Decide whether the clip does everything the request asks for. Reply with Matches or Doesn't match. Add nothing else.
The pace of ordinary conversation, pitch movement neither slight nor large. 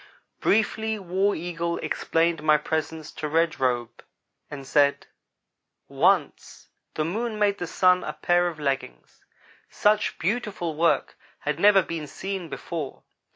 Doesn't match